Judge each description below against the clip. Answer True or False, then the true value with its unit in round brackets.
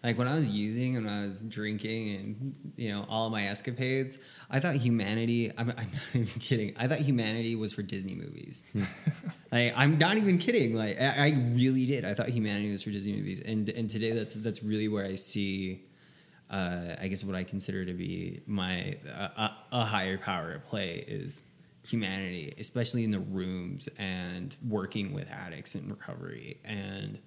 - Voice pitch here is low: True (110 Hz)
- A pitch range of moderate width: True (3.9 semitones)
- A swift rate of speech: False (185 wpm)